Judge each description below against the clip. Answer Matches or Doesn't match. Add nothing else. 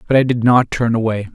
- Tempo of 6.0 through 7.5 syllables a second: Matches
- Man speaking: Matches